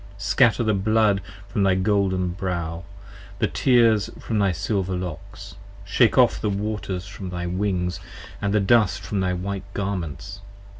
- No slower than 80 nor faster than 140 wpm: No, average, 155 wpm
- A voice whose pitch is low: Yes, low, 100 Hz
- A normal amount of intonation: No, narrow, 2.3 semitones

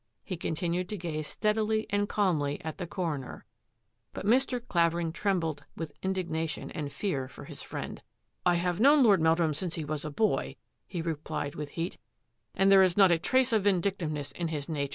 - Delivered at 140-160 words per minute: No, average, 195 wpm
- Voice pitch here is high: No, medium, 170 Hz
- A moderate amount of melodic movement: Yes, average, 4.1 semitones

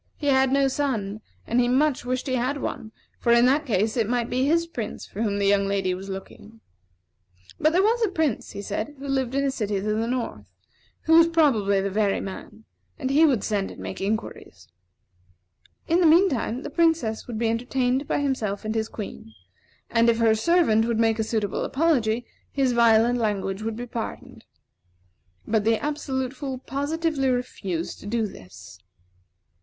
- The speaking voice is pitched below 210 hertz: No, high, 235 Hz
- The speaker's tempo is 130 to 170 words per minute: No, average, 190 wpm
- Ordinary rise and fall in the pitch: Yes, average, 4.3 semitones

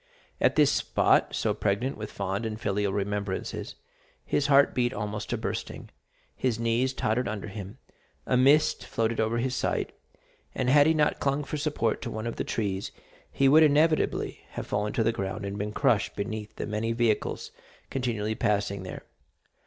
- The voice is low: Yes, low, 115 Hz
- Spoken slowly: No, average, 175 wpm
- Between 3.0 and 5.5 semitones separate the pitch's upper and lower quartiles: Yes, average, 4.2 semitones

